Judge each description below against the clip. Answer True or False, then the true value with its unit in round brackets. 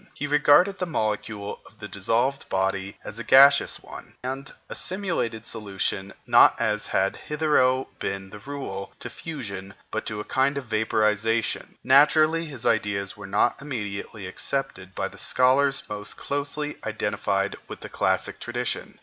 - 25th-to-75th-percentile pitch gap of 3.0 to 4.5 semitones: False (5.6 semitones)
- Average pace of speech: True (150 wpm)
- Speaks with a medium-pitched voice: False (115 Hz)